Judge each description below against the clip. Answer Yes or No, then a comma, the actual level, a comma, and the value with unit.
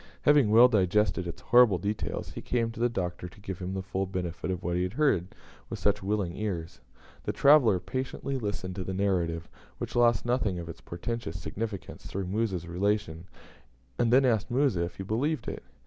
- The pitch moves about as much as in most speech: Yes, average, 4.6 semitones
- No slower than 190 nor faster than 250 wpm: Yes, average, 195 wpm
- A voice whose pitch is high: No, low, 100 Hz